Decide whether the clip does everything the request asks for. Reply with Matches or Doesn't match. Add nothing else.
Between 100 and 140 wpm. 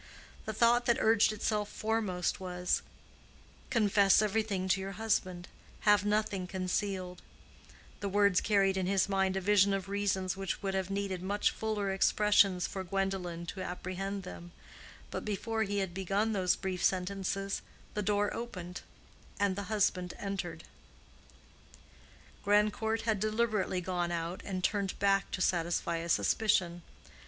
Matches